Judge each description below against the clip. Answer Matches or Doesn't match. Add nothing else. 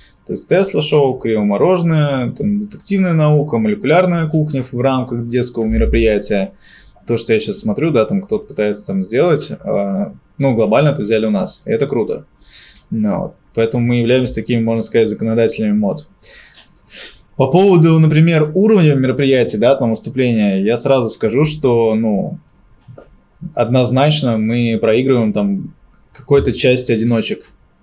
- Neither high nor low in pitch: Doesn't match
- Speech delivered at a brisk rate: Doesn't match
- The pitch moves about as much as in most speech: Doesn't match